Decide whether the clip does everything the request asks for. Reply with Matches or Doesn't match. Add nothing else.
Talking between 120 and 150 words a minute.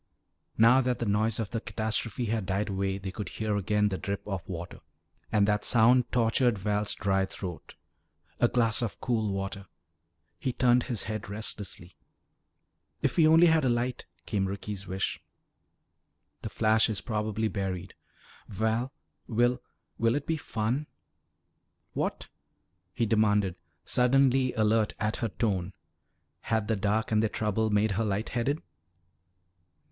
Matches